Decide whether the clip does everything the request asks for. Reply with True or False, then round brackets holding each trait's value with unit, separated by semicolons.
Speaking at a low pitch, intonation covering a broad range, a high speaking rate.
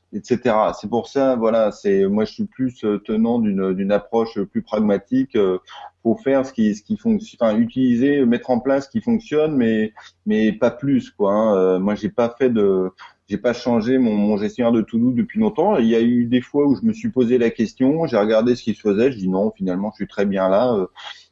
True (120 Hz; 6.5 semitones; 230 wpm)